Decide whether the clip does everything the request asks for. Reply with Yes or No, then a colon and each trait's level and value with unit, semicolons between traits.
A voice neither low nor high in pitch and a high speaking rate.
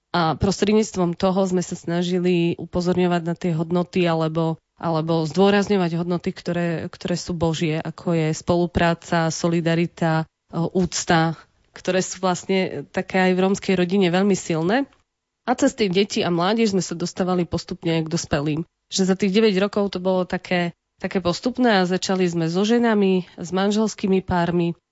No: medium, 180 Hz; average, 150 wpm